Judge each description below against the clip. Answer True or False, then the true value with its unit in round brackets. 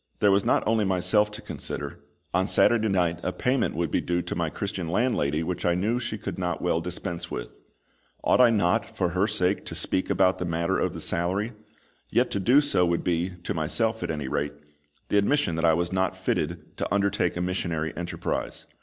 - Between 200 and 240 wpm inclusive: True (205 wpm)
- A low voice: True (90 Hz)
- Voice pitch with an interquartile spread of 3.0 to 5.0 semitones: True (3.4 semitones)